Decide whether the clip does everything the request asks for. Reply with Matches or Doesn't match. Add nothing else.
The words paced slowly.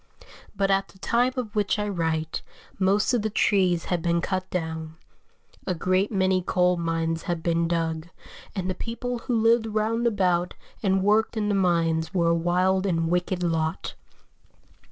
Doesn't match